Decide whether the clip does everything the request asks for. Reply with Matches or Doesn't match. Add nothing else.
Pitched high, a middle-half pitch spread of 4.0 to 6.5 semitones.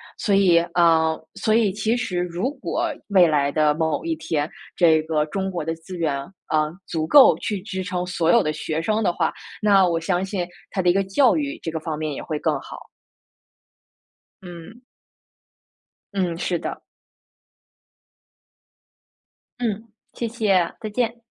Doesn't match